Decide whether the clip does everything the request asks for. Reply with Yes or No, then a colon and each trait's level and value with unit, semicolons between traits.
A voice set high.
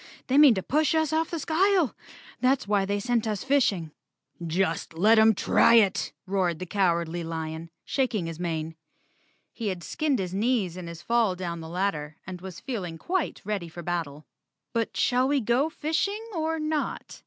Yes: high, 200 Hz